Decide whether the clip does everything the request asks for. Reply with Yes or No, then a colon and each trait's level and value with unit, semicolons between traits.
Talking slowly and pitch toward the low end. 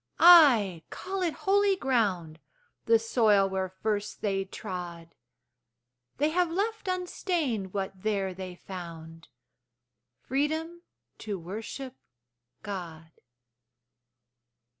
No: slow, 95 wpm; high, 210 Hz